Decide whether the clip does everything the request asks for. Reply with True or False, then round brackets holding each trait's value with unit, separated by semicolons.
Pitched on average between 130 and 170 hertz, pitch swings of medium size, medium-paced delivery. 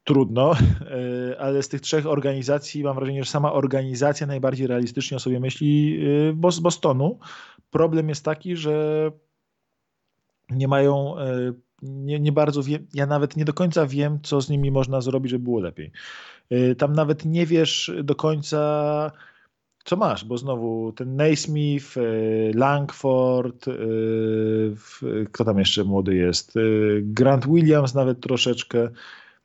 True (135 Hz; 3.2 semitones; 130 wpm)